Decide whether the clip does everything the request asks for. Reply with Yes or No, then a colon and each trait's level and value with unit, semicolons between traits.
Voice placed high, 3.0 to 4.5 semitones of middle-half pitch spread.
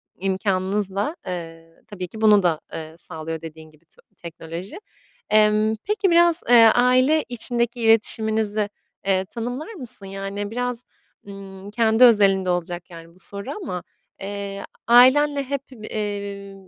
Yes: high, 205 Hz; average, 4.2 semitones